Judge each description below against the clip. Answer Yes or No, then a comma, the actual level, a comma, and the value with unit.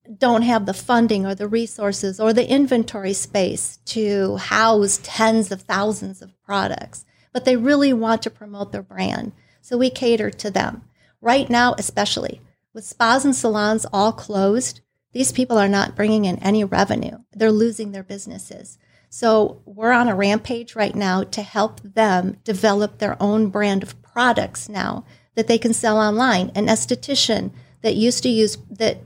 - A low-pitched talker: No, high, 220 Hz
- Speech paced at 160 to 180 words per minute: Yes, average, 165 wpm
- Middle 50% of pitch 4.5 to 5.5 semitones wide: No, narrow, 2.5 semitones